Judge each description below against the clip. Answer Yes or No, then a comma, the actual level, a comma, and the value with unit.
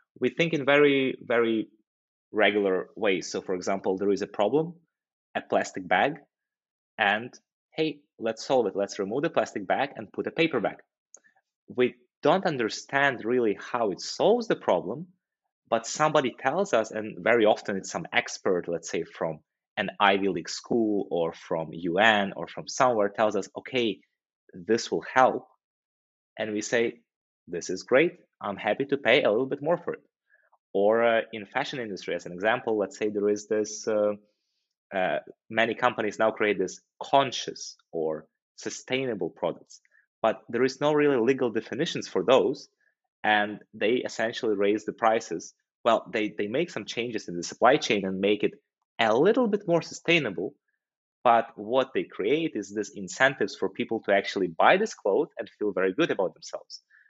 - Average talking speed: Yes, average, 170 wpm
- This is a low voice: Yes, low, 115 Hz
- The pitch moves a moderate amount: No, wide, 5.7 semitones